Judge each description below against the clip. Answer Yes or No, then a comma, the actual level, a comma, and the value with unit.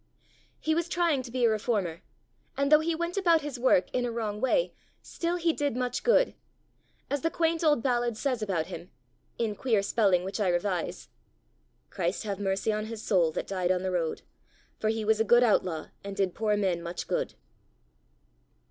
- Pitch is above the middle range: Yes, high, 220 Hz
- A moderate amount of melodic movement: No, wide, 6.5 semitones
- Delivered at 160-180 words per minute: No, average, 190 wpm